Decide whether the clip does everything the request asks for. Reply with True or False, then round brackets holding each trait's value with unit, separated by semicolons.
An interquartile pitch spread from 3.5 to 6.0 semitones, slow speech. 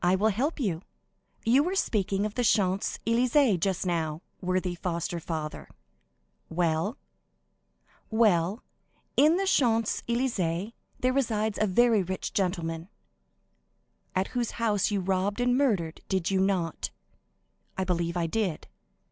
True (4.7 semitones; 130 wpm)